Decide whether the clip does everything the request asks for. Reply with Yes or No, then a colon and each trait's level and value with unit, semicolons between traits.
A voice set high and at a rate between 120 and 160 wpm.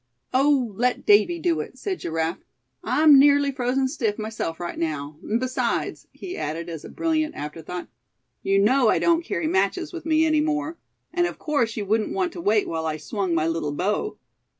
No: high, 245 Hz; average, 195 wpm